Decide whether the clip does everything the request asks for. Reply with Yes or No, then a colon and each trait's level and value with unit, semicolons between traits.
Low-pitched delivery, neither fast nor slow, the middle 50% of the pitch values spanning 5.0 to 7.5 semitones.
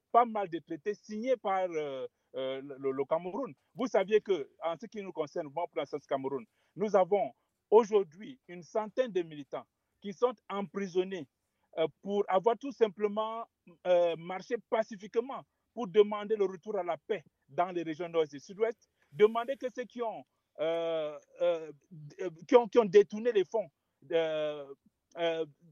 No: medium, 185 Hz; average, 155 wpm; wide, 5.5 semitones